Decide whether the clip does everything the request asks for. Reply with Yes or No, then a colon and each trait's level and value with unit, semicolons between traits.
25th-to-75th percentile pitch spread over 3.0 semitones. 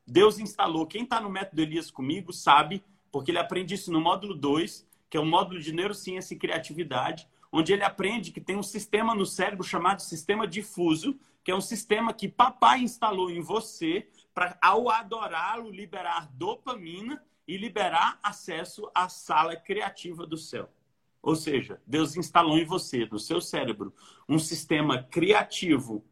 Yes: average, 3.9 semitones